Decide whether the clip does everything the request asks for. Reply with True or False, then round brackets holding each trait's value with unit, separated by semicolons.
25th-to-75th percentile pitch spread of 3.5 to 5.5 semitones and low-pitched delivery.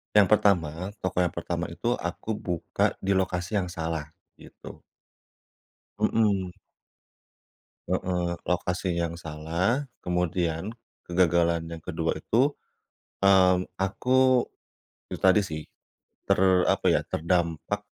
False (2.7 semitones; 90 Hz)